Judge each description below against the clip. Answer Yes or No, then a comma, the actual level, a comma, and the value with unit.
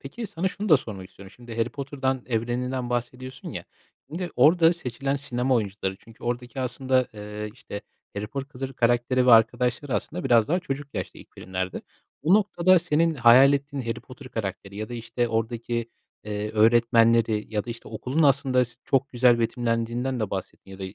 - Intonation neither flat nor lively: Yes, average, 3.2 semitones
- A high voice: No, low, 120 Hz